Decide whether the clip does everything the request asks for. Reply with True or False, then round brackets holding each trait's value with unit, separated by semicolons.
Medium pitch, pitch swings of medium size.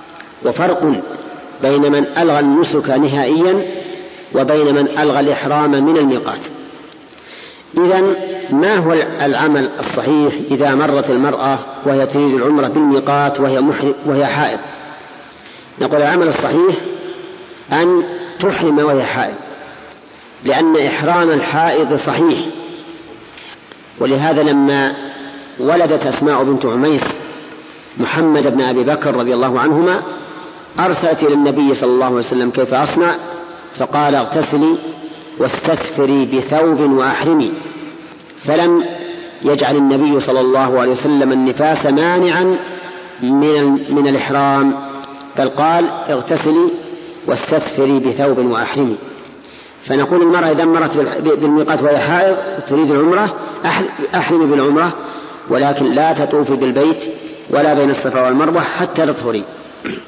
True (145 Hz; 3.1 semitones)